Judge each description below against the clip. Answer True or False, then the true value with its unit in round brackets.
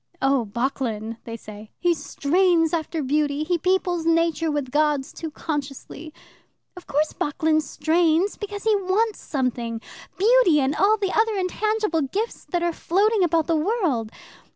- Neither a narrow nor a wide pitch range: True (4.9 semitones)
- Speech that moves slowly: False (150 wpm)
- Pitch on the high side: True (325 Hz)